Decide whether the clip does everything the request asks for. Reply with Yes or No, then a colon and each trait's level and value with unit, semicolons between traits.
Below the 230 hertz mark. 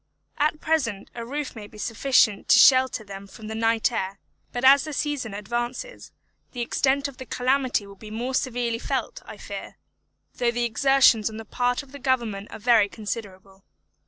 No: high, 235 Hz